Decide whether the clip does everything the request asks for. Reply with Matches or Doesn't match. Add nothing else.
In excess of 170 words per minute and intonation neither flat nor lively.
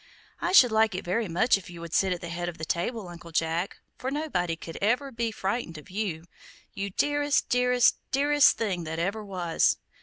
Doesn't match